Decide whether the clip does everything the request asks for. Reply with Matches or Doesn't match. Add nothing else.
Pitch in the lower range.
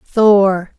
Doesn't match